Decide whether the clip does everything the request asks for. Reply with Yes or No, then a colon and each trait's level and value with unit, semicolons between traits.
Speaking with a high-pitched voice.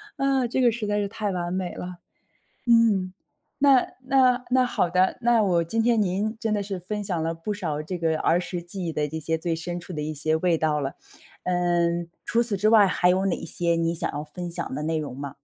No: medium, 180 Hz